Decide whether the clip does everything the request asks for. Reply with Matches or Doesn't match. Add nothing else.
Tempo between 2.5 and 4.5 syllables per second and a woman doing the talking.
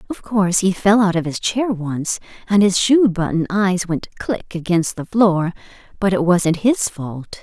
Matches